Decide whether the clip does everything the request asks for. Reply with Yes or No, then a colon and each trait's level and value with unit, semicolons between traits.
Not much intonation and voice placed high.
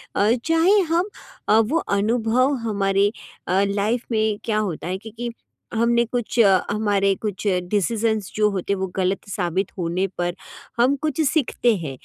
No: average, 3.4 semitones; high, 215 Hz